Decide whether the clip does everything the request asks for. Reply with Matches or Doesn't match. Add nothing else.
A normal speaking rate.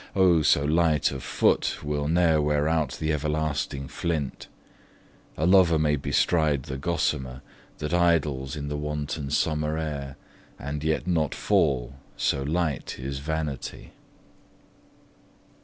Doesn't match